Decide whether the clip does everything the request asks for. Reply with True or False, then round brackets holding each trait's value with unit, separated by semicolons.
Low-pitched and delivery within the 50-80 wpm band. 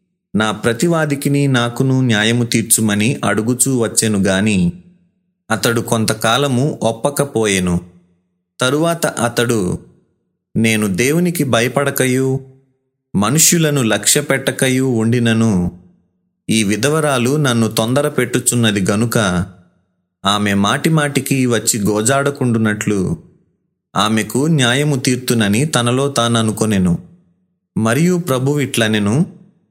True (125 Hz; 75 wpm)